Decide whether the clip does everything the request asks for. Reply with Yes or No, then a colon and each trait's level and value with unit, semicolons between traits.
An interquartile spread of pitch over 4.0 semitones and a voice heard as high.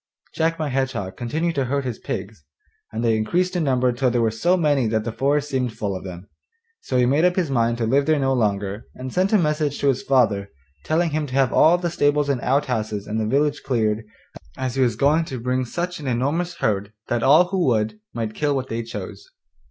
No: average, 4.8 semitones; low, 130 Hz